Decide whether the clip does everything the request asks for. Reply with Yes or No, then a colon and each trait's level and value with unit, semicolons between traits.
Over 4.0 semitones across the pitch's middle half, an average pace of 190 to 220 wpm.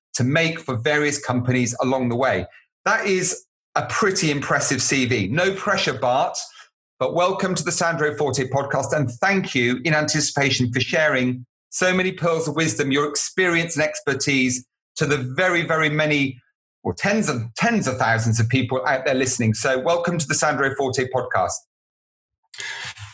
No: average, 4.6 semitones; average, 165 wpm